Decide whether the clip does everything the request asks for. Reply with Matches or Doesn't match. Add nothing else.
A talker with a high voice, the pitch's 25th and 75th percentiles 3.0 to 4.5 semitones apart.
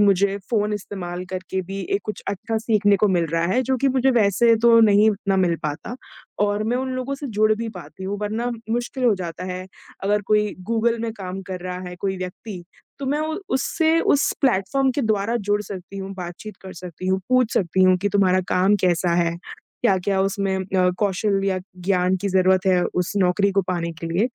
Matches